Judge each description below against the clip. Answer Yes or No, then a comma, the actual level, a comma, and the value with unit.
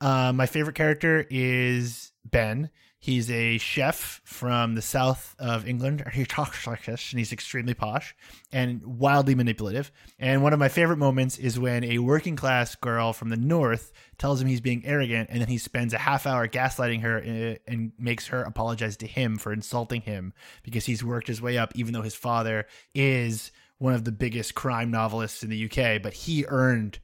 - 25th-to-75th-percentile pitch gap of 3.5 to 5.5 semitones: No, narrow, 2.5 semitones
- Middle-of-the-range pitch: No, low, 120 Hz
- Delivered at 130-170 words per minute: No, average, 190 wpm